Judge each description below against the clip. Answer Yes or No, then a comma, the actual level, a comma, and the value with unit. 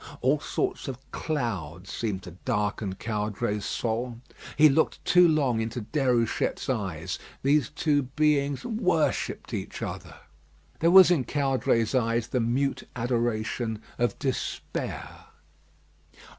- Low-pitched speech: Yes, low, 125 Hz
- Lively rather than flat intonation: No, average, 4.5 semitones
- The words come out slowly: Yes, slow, 115 wpm